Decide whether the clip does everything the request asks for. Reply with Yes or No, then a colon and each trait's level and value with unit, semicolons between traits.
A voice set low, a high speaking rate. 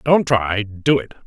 No: low, 120 Hz; average, 140 wpm